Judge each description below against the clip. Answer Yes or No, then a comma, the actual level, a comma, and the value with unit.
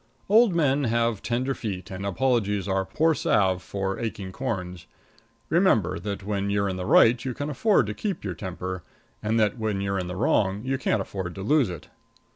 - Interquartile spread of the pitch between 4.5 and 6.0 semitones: Yes, average, 5.2 semitones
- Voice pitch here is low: Yes, low, 105 Hz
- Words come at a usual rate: Yes, average, 195 wpm